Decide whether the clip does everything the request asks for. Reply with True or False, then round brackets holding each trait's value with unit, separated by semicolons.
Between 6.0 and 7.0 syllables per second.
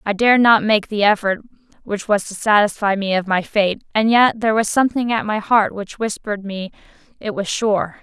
False (5.4 syllables/s)